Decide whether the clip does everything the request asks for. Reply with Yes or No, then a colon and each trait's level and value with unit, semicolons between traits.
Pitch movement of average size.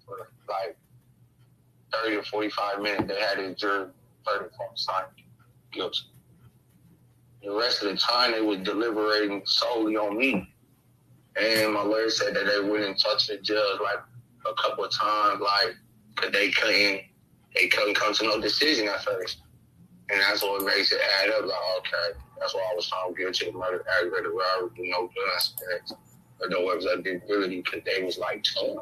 No: narrow, 2.3 semitones